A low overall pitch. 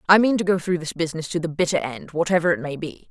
No: medium, 170 Hz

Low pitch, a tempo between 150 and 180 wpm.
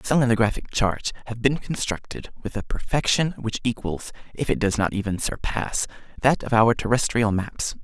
Yes: low, 115 Hz; average, 160 wpm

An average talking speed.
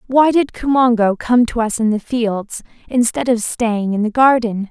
Yes: average, 190 wpm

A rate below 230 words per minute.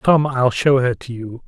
No: fast, 245 wpm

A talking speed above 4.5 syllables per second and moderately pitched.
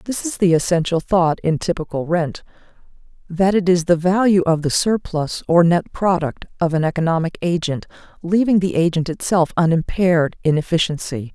Yes: 5.1 syllables/s; medium, 170 Hz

